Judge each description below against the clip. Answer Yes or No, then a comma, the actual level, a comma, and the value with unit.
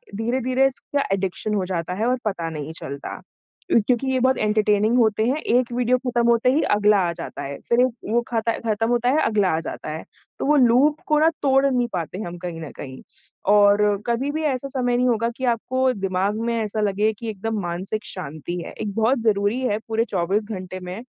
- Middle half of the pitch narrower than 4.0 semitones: No, average, 4.4 semitones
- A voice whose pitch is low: No, high, 220 Hz